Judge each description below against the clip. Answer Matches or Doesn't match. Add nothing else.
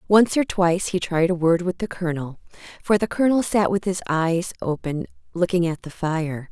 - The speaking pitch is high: Doesn't match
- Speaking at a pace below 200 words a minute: Doesn't match